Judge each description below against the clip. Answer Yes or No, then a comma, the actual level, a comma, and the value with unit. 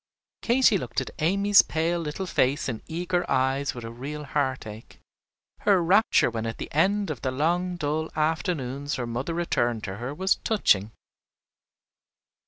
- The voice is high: No, medium, 150 Hz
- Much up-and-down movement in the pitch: Yes, wide, 5.7 semitones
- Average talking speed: Yes, average, 155 wpm